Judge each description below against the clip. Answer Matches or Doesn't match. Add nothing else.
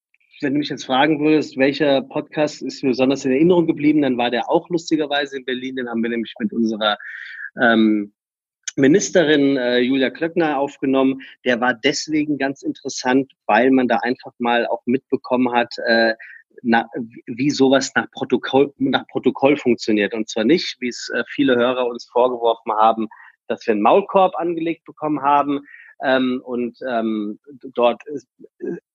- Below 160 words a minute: Doesn't match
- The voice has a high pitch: Doesn't match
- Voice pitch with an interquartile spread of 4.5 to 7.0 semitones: Doesn't match